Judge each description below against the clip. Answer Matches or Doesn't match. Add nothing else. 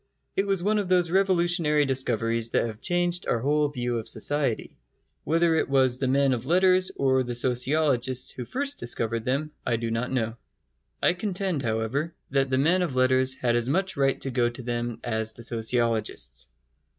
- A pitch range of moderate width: Doesn't match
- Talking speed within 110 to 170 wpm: Doesn't match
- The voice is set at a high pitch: Doesn't match